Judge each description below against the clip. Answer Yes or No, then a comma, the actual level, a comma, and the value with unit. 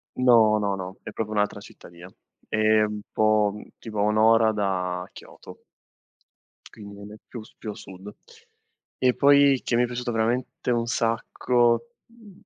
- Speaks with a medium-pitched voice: No, low, 110 Hz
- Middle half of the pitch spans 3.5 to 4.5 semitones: No, average, 2.7 semitones